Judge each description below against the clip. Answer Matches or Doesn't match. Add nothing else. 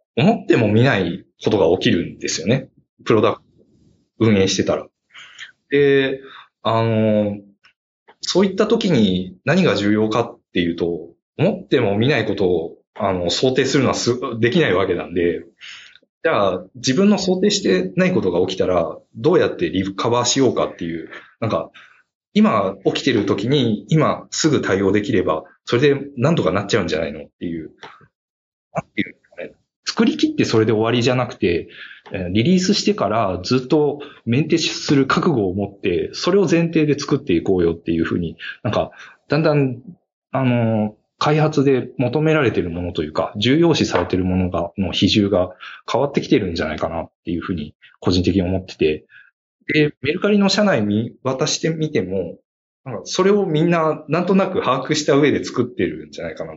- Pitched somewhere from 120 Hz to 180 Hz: Matches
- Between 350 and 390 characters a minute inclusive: Doesn't match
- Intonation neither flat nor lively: Doesn't match